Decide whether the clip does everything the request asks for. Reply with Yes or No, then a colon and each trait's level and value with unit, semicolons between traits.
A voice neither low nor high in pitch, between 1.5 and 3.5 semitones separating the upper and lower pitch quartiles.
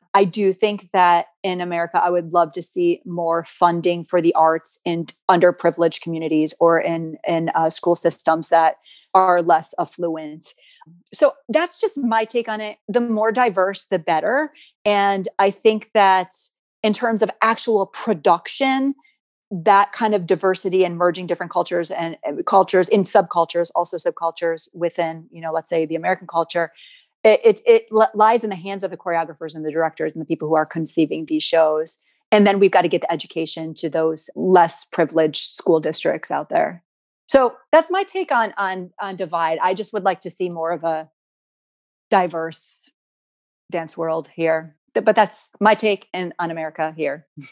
No: medium, 175 Hz; average, 4.2 semitones